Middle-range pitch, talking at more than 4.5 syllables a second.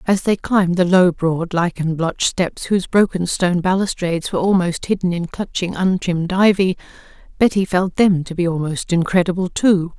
Yes: medium, 180 Hz; 5.3 syllables/s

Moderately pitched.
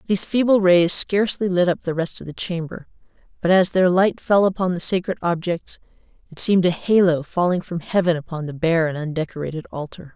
Yes: medium, 175 Hz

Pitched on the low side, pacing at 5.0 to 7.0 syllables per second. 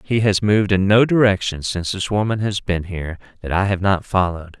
Yes: very low, 95 Hz; 5.9 syllables/s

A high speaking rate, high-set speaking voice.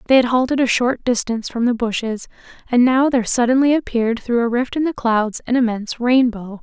Yes: fast, 210 wpm; high, 240 Hz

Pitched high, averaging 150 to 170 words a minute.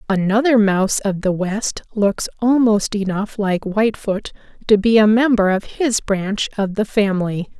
Yes: high, 205 Hz; average, 160 wpm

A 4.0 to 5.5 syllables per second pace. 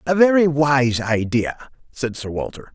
Yes: 4.1 syllables/s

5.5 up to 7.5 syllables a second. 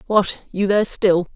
No: 4.8 syllables/s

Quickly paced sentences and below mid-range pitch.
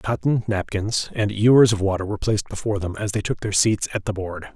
Yes: fast, 235 wpm; low, 105 Hz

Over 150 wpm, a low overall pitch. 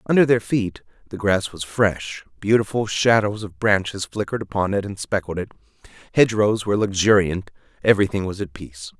Yes: average, 160 wpm; low, 100 Hz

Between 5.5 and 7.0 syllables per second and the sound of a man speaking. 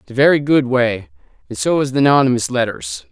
Yes: 5.6 syllables/s; male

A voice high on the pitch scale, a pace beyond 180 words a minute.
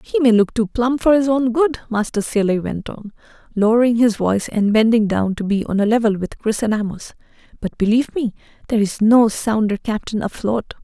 Yes: high, 225 Hz; average, 200 wpm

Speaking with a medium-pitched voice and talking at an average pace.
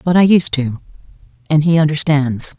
Yes: medium, 150 Hz; average, 165 wpm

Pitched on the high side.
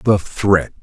No: very low, 95 Hz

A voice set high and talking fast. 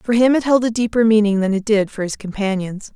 Yes: high, 215 Hz; fast, 265 wpm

